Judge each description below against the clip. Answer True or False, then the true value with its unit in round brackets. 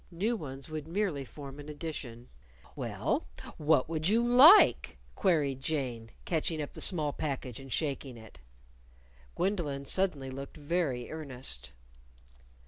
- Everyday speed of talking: False (130 wpm)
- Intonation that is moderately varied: True (3.8 semitones)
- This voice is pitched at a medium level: True (145 Hz)